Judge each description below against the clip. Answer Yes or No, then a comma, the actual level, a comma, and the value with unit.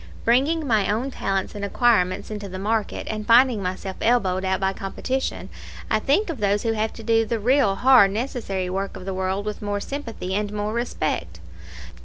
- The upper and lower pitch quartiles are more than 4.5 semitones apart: No, average, 3.7 semitones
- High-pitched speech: Yes, high, 210 Hz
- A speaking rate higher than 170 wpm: Yes, average, 190 wpm